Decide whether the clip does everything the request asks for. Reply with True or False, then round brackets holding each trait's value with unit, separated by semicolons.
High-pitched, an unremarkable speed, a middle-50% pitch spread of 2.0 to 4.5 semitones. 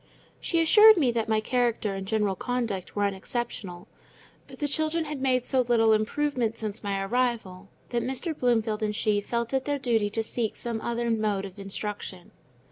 True (230 Hz; 180 wpm; 3.5 semitones)